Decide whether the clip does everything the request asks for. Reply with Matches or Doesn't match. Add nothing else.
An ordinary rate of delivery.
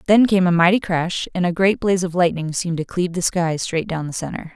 Doesn't match